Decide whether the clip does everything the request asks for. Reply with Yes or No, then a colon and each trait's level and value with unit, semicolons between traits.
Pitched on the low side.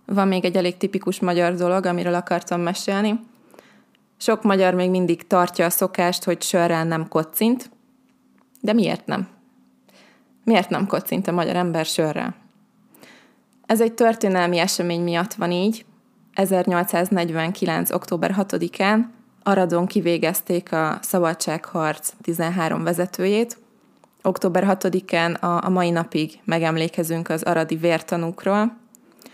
No: medium, 180 Hz